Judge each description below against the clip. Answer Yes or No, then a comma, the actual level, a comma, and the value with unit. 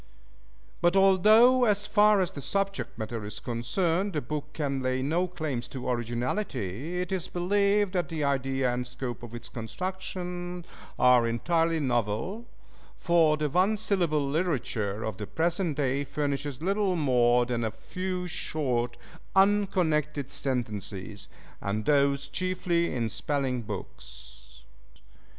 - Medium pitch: Yes, medium, 145 Hz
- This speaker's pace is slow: Yes, slow, 130 wpm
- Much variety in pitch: Yes, wide, 6.8 semitones